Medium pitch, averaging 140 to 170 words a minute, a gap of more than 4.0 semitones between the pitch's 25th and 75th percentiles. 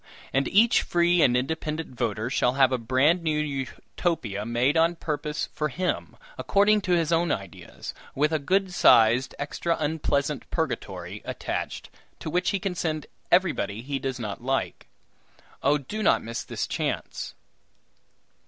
Yes: medium, 150 Hz; average, 150 wpm; average, 4.9 semitones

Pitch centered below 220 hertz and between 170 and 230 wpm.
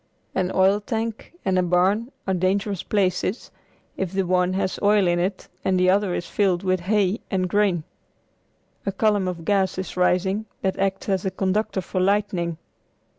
Yes: high, 190 Hz; average, 175 wpm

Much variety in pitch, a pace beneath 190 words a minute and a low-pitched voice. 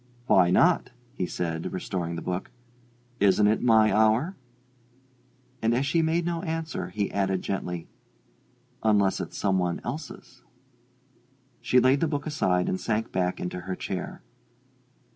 Yes: wide, 7.0 semitones; average, 145 wpm; low, 105 Hz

